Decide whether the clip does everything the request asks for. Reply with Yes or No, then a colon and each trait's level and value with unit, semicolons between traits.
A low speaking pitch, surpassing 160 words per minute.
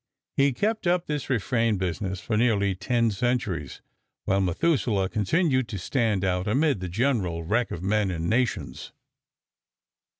No: low, 110 Hz; average, 140 wpm